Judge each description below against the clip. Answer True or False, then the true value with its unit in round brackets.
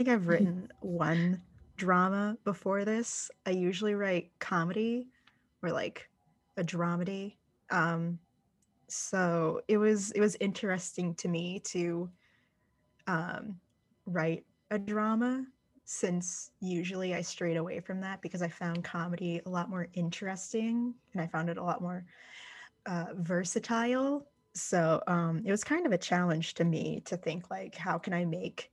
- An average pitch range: True (3.3 semitones)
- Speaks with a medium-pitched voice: True (180 Hz)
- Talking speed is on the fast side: False (145 wpm)